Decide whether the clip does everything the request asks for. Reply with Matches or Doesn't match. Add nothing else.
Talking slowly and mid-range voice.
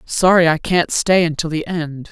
Doesn't match